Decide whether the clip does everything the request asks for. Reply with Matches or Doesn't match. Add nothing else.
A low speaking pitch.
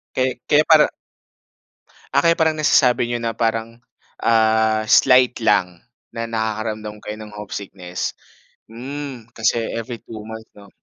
Matches